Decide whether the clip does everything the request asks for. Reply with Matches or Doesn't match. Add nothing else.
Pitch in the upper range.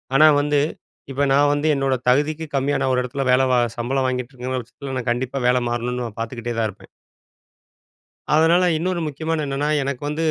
Doesn't match